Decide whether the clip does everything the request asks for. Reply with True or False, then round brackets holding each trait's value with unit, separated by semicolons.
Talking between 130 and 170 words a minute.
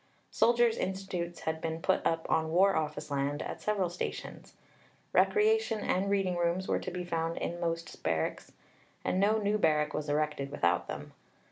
True (165 wpm)